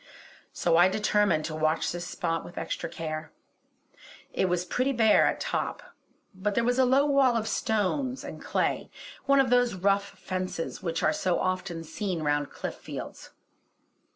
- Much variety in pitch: Yes, wide, 6.0 semitones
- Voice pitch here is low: No, high, 190 Hz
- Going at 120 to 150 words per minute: No, average, 165 wpm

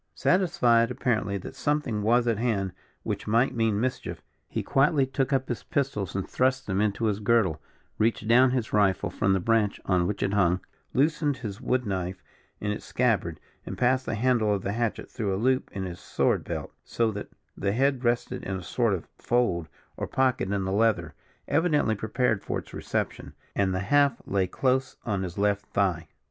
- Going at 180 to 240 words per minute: Yes, average, 190 wpm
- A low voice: Yes, low, 110 Hz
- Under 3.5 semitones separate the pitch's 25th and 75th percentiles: No, average, 4.4 semitones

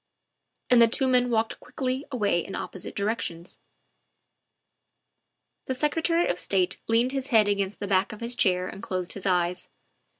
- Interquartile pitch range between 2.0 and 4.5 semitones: No, average, 5.2 semitones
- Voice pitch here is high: Yes, high, 215 Hz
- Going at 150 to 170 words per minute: Yes, average, 160 wpm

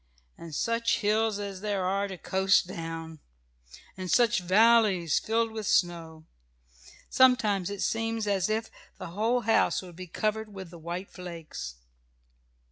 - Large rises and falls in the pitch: No, average, 4.0 semitones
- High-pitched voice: Yes, high, 195 Hz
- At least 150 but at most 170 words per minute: No, average, 140 wpm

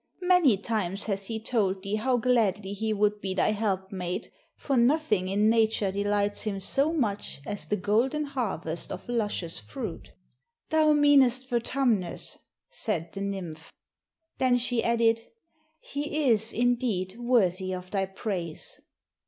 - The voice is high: Yes, high, 215 Hz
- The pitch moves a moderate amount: Yes, average, 4.2 semitones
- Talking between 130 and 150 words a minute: Yes, slow, 135 wpm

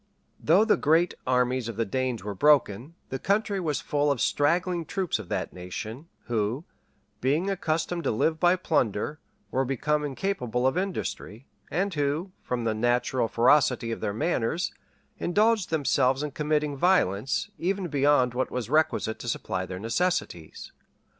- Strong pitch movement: Yes, wide, 6.1 semitones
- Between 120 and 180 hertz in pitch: Yes, medium, 140 Hz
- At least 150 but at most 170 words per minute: Yes, average, 155 wpm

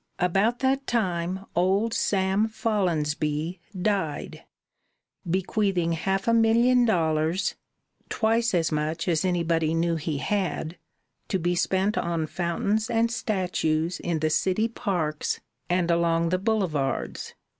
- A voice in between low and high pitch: Yes, medium, 180 Hz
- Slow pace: Yes, slow, 120 wpm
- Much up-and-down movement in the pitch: No, average, 4.3 semitones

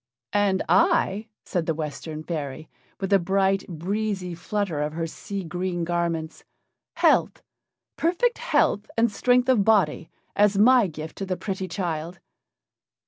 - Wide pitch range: No, average, 4.0 semitones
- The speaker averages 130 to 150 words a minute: Yes, average, 140 wpm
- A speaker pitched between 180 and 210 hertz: Yes, high, 190 Hz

